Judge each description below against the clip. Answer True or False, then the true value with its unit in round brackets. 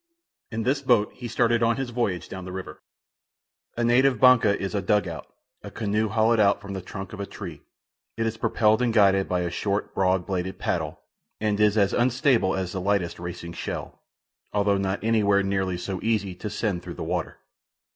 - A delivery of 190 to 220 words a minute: True (200 wpm)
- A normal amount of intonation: True (3.1 semitones)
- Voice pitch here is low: True (100 Hz)